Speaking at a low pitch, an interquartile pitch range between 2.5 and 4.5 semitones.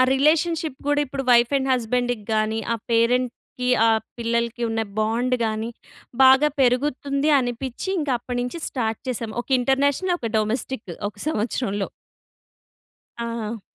No: high, 245 Hz; average, 2.9 semitones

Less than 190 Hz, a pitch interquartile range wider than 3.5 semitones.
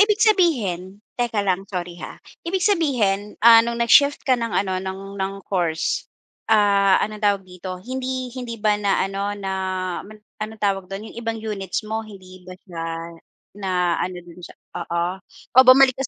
No: high, 205 Hz; average, 4.0 semitones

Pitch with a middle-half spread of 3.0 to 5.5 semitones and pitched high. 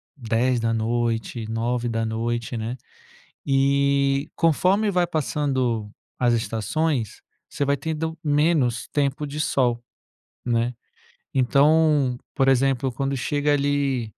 No: average, 3.6 semitones; low, 135 Hz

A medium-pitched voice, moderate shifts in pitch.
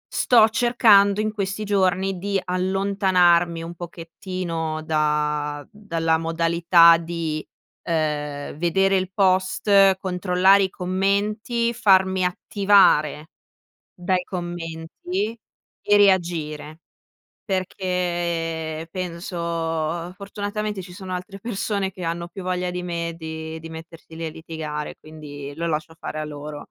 Yes: medium, 180 Hz; average, 3.1 semitones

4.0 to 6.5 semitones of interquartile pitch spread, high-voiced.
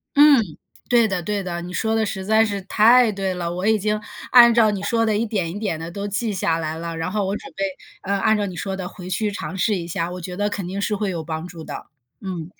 No: average, 3.3 semitones; high, 195 Hz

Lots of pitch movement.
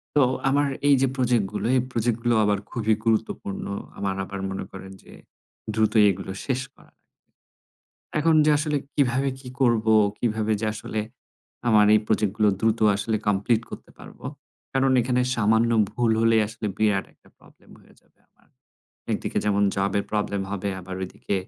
No: average, 3.0 semitones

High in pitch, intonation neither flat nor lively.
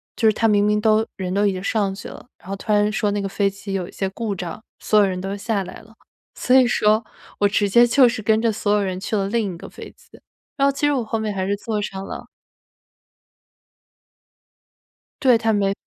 No: high, 210 Hz; narrow, 2.2 semitones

